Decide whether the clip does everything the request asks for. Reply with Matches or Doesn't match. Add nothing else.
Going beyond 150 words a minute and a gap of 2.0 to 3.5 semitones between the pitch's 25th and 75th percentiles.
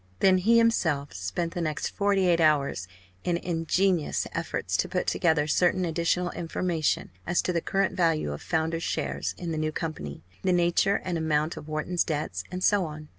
Matches